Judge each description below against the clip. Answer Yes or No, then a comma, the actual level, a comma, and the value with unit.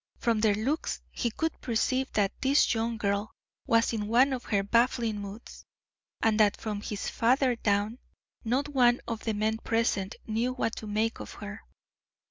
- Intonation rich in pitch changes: No, narrow, 2.5 semitones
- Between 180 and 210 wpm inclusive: No, average, 170 wpm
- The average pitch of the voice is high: Yes, high, 225 Hz